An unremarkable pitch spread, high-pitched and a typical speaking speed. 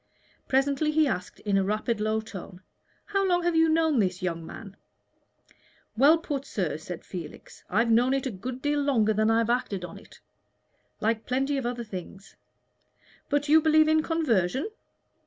No: wide, 6.5 semitones; high, 240 Hz; average, 175 wpm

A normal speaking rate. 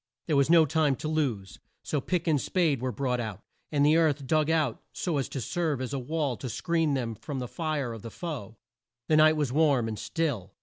No: fast, 225 wpm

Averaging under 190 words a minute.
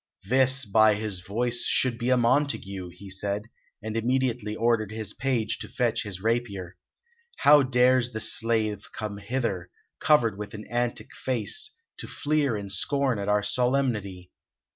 Yes: average, 150 wpm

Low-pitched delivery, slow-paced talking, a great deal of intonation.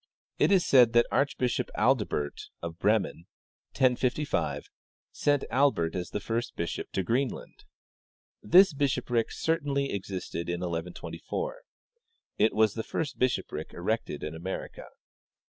Yes: low, 115 Hz; slow, 125 wpm; wide, 7.3 semitones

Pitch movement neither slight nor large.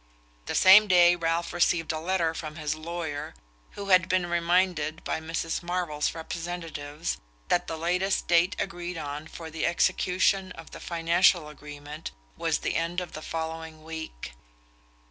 No: narrow, 2.0 semitones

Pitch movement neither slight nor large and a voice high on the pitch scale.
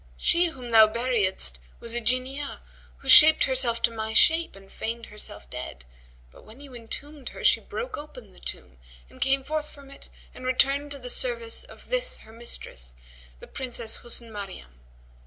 Yes: average, 4.3 semitones; high, 245 Hz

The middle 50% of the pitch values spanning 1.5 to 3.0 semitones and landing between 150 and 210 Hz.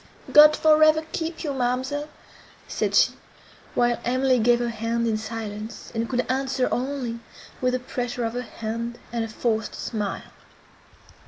No: narrow, 2.6 semitones; high, 245 Hz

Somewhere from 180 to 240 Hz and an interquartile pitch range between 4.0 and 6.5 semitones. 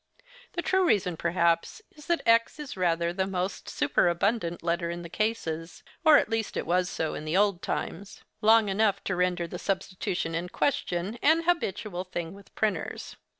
Yes: medium, 185 Hz; average, 4.3 semitones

